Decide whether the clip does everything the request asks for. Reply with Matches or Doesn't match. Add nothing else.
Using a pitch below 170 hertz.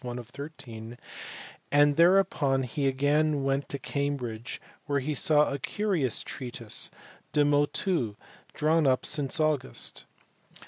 Matches